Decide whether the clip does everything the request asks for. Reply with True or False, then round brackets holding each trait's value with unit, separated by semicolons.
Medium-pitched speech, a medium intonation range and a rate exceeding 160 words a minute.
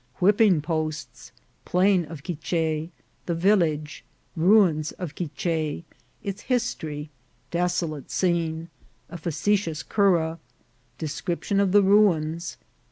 False (165 Hz; 3.5 semitones; 135 wpm)